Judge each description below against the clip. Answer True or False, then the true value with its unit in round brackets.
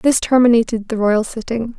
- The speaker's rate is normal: True (170 wpm)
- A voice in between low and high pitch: False (230 Hz)